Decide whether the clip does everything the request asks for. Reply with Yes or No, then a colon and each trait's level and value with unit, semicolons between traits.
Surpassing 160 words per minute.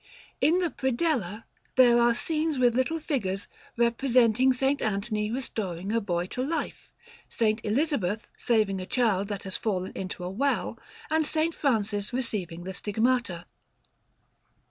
No: average, 140 wpm